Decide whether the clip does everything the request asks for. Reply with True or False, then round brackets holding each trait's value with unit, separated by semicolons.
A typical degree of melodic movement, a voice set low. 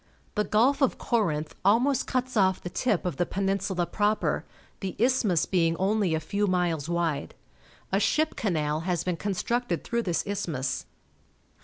False (4.2 semitones; 195 Hz)